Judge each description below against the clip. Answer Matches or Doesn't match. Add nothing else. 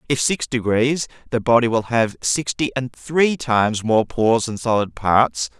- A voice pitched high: Doesn't match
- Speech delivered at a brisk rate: Doesn't match